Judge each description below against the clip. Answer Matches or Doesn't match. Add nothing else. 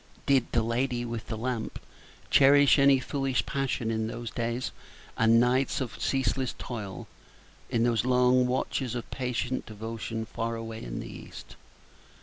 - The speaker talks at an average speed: Matches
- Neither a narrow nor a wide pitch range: Doesn't match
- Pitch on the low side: Matches